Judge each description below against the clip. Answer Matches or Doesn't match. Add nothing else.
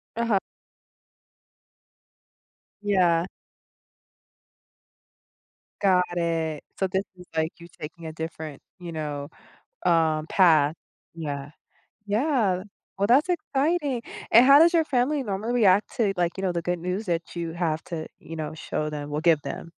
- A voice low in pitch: Doesn't match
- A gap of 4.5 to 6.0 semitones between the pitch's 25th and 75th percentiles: Matches